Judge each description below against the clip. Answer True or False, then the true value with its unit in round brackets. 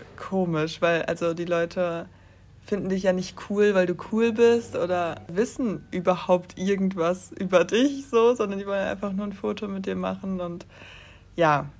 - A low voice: False (185 Hz)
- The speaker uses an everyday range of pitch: True (3.5 semitones)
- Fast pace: False (170 wpm)